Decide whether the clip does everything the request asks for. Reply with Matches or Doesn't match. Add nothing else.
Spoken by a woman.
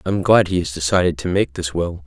Doesn't match